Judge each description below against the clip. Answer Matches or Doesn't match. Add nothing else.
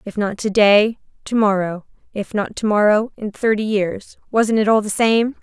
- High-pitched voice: Matches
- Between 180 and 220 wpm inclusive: Doesn't match